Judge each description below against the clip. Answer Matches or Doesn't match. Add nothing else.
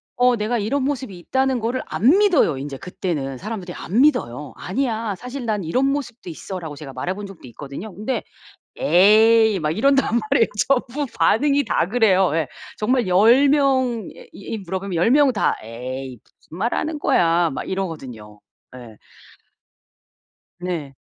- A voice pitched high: Matches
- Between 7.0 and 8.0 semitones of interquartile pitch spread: Matches